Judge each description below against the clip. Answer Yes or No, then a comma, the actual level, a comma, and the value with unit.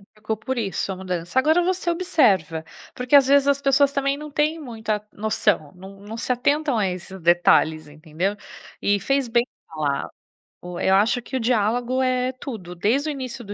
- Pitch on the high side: Yes, high, 225 Hz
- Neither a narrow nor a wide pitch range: No, wide, 6.4 semitones